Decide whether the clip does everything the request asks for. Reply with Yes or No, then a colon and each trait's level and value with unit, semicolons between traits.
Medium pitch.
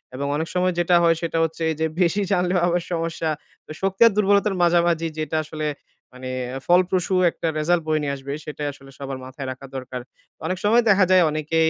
Yes: medium, 165 Hz